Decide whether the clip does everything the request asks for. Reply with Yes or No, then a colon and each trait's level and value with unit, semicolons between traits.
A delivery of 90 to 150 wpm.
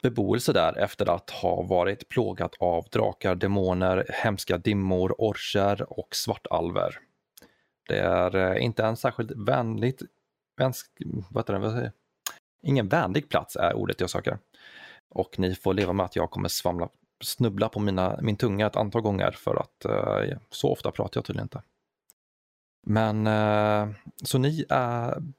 Yes: average, 140 wpm